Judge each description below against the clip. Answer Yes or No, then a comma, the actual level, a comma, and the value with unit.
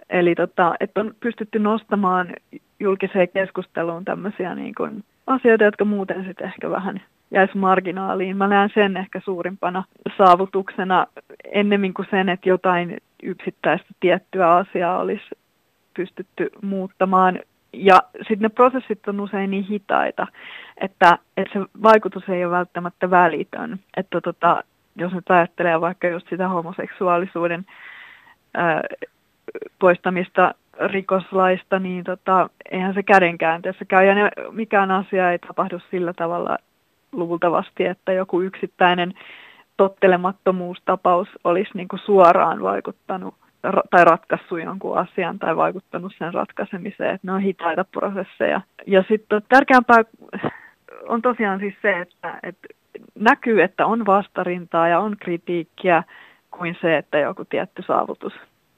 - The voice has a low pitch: No, high, 190 Hz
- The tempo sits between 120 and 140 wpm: Yes, average, 125 wpm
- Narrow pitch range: Yes, narrow, 2.2 semitones